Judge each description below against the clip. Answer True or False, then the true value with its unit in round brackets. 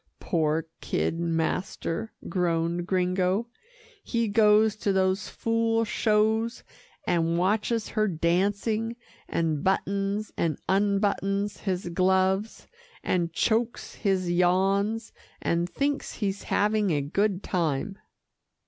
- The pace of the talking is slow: True (105 wpm)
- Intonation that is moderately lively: True (3.5 semitones)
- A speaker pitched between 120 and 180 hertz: False (195 Hz)